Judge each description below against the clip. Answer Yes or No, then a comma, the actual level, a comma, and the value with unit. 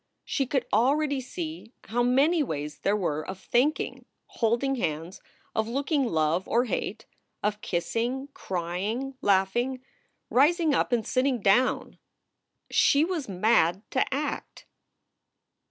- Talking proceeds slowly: Yes, slow, 120 wpm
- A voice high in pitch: Yes, high, 240 Hz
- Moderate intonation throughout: No, wide, 6.1 semitones